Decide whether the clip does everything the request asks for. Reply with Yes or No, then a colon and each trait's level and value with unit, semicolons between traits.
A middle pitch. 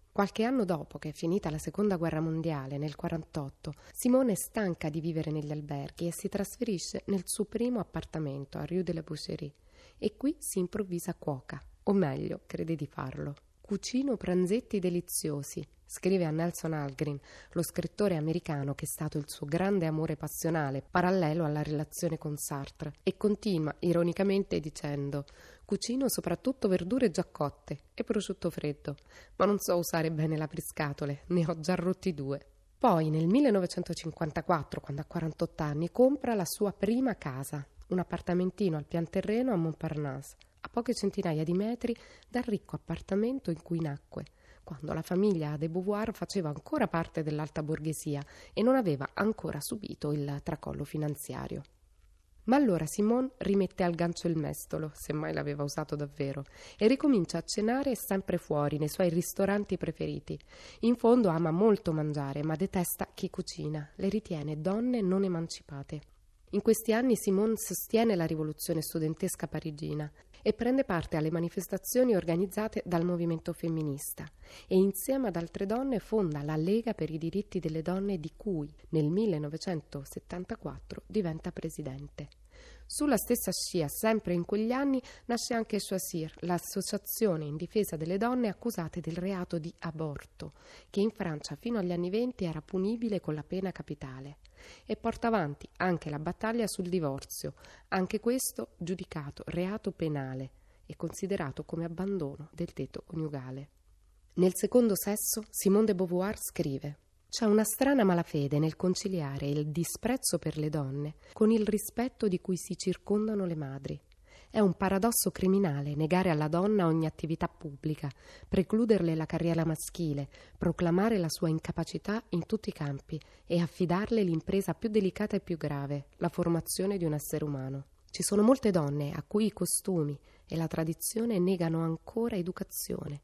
Yes: medium, 175 Hz